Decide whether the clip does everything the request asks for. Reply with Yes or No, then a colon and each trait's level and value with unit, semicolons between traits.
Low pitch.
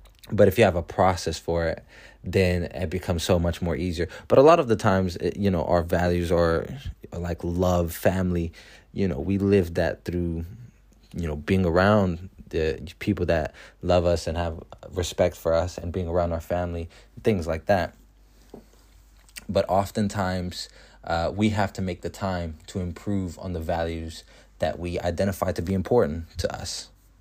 Yes: very low, 90 Hz